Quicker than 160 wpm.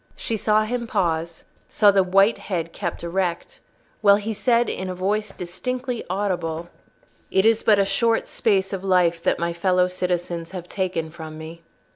Yes: average, 170 wpm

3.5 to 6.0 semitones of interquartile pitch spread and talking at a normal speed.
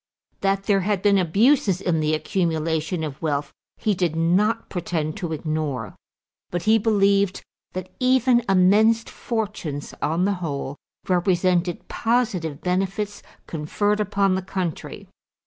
No: average, 4.2 semitones; slow, 130 wpm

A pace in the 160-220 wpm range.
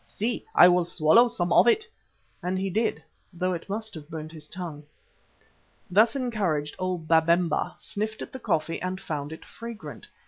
Yes: average, 170 wpm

